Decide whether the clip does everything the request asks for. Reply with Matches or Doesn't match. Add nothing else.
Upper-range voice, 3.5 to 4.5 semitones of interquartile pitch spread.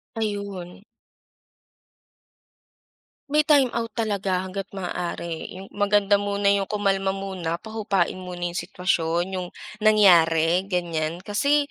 Doesn't match